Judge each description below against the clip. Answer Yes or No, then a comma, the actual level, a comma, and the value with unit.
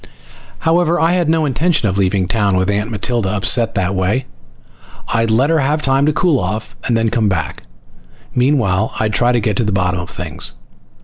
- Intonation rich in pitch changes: Yes, wide, 6.3 semitones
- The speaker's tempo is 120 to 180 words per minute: No, average, 190 wpm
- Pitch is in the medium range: No, low, 115 Hz